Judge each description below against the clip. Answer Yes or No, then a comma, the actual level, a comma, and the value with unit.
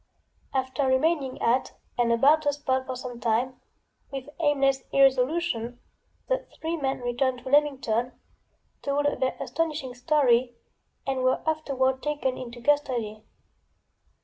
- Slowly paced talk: Yes, slow, 120 wpm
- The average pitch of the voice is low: No, very high, 260 Hz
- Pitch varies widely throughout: No, average, 2.8 semitones